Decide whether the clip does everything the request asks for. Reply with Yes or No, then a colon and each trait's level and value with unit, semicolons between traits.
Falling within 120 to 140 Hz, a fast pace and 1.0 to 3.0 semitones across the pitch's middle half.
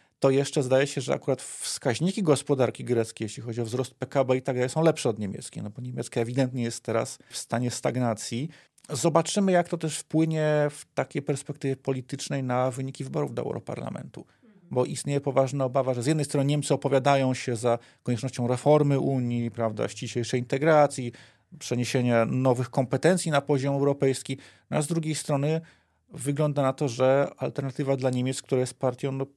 Yes: low, 135 Hz; fast, 170 wpm; average, 2.7 semitones